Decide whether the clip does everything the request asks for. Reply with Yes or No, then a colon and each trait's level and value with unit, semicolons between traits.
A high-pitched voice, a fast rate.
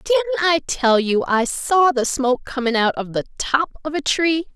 Yes: very high, 280 Hz; fast, 210 wpm